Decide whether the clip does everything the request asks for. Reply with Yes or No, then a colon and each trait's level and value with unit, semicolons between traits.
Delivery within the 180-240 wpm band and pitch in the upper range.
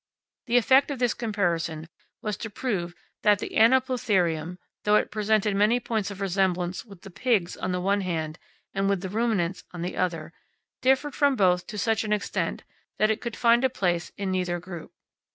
Yes: average, 190 wpm; high, 200 Hz